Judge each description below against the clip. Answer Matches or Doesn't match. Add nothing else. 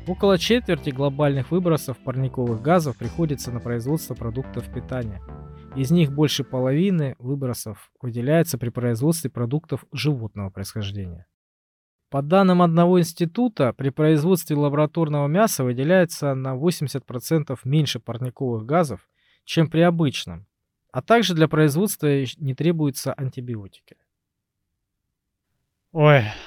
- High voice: Doesn't match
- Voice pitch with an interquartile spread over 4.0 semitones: Matches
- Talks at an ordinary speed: Doesn't match